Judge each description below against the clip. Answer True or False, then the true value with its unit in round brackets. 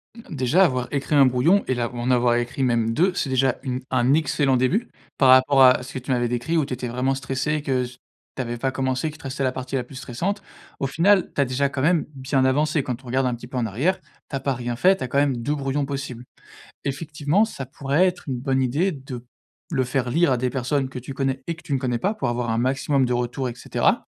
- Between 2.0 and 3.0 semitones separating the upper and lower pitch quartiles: True (2.4 semitones)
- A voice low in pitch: True (130 Hz)